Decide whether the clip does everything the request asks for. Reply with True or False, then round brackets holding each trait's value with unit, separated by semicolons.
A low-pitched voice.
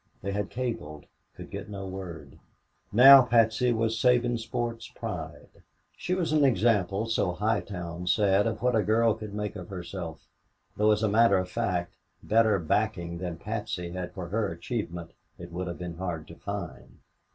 True (100 Hz)